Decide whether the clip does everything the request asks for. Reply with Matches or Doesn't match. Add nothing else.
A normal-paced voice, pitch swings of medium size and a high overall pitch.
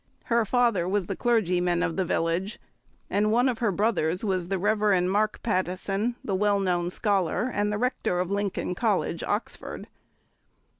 Matches